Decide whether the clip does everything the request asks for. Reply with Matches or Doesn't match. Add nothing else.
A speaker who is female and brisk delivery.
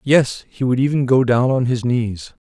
Doesn't match